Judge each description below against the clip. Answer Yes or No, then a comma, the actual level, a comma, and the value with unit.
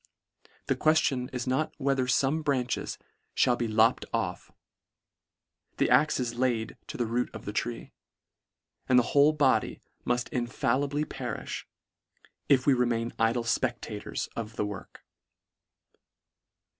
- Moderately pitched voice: No, low, 125 Hz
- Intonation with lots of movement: No, average, 2.7 semitones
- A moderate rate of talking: No, slow, 130 wpm